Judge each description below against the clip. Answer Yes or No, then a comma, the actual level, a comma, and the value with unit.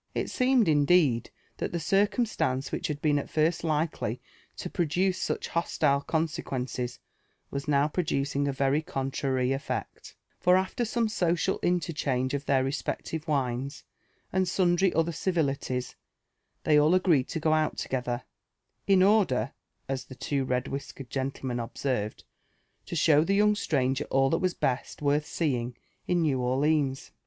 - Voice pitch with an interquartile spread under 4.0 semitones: No, average, 4.5 semitones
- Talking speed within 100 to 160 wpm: Yes, average, 145 wpm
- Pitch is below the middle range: No, medium, 145 Hz